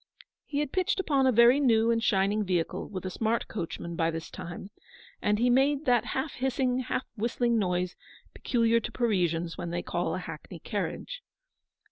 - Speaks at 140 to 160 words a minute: No, average, 175 wpm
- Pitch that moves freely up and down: Yes, wide, 5.8 semitones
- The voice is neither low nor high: No, high, 230 Hz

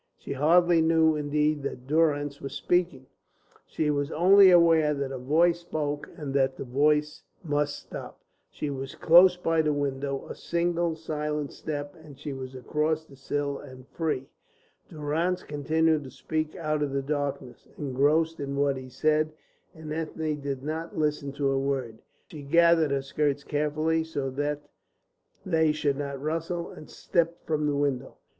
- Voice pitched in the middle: Yes, medium, 150 Hz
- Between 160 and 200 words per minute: Yes, average, 165 wpm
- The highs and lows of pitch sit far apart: No, narrow, 2.4 semitones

